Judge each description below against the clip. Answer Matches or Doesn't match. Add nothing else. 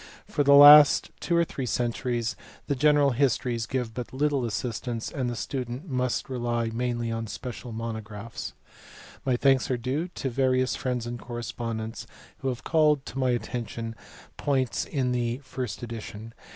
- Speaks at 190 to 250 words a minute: Doesn't match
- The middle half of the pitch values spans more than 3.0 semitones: Doesn't match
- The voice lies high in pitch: Doesn't match